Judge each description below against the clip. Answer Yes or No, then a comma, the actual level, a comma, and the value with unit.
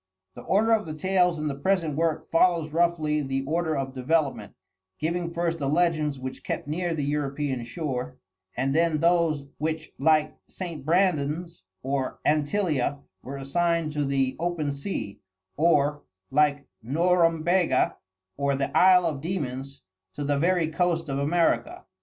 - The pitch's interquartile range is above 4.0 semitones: No, average, 3.4 semitones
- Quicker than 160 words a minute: No, average, 145 wpm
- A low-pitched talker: No, medium, 155 Hz